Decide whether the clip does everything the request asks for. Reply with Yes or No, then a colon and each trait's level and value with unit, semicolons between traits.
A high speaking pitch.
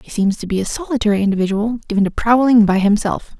Yes: high, 215 Hz